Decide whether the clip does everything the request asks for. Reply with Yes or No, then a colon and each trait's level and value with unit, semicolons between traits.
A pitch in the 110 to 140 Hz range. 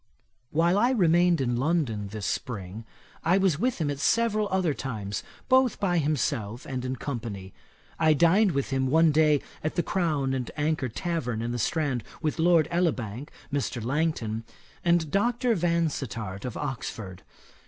No: medium, 150 Hz